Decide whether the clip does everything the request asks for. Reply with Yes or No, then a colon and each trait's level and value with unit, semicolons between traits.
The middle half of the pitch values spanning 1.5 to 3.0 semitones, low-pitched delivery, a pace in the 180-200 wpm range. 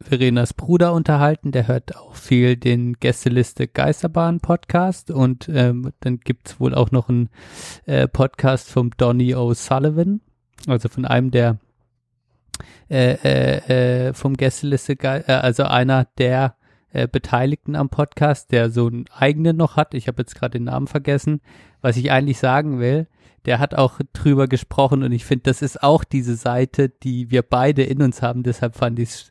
No: narrow, 2.4 semitones; low, 130 Hz; average, 165 wpm